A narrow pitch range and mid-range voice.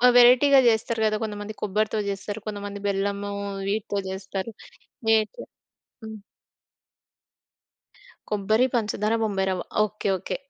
No: narrow, 1.5 semitones; high, 210 Hz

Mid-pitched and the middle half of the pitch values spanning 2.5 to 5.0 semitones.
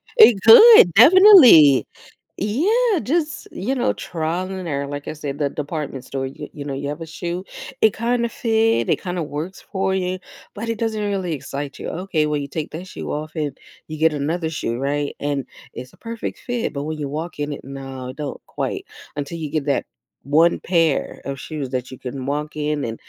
No: medium, 155 Hz; wide, 5.4 semitones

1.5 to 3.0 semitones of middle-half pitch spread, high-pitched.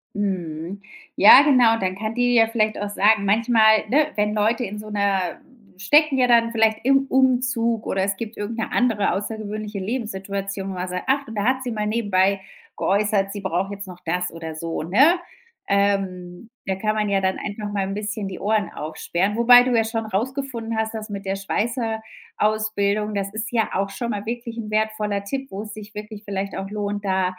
Yes: narrow, 2.5 semitones; high, 210 Hz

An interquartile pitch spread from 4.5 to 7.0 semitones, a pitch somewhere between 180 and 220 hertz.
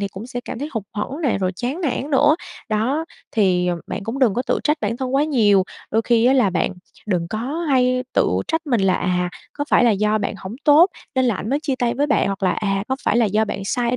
No: average, 5.2 semitones; high, 235 Hz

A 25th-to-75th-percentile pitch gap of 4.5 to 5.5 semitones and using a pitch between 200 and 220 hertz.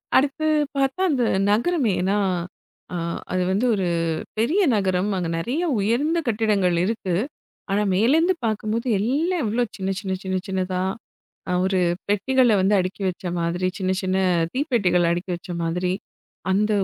Yes: average, 5.2 semitones; high, 205 Hz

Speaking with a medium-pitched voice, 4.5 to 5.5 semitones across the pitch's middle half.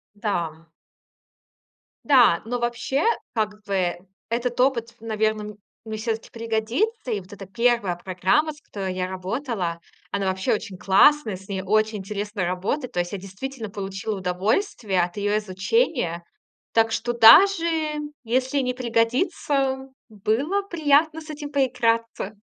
No: high, 220 Hz; average, 5.0 semitones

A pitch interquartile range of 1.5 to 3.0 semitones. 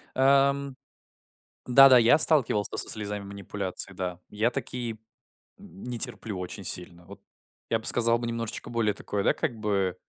No: average, 3.8 semitones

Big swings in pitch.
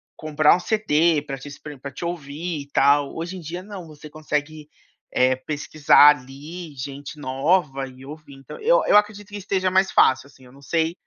No: average, 3.9 semitones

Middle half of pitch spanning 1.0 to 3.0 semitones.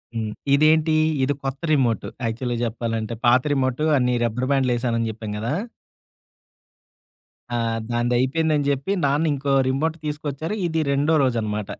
No: average, 3.7 semitones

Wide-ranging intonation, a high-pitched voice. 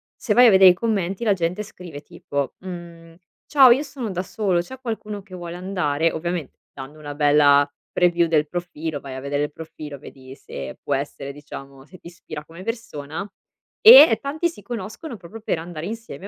No: wide, 6.0 semitones; medium, 175 Hz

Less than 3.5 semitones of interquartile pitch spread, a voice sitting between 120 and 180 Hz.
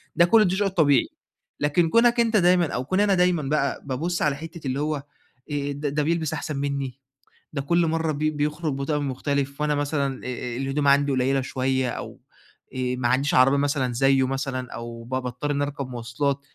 Yes: average, 2.8 semitones; medium, 140 Hz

